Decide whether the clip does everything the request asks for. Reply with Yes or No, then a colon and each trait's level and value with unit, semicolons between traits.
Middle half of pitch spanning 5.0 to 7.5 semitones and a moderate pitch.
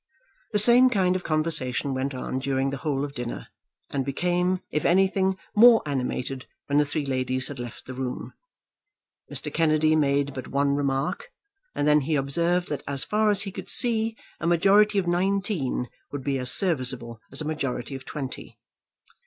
Yes: wide, 5.4 semitones; medium, 145 Hz